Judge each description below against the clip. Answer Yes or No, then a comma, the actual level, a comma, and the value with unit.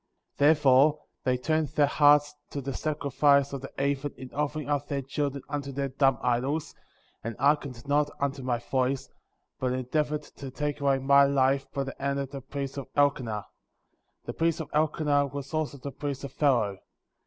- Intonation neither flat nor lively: No, narrow, 1.5 semitones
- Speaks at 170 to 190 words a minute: Yes, average, 180 wpm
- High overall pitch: No, medium, 140 Hz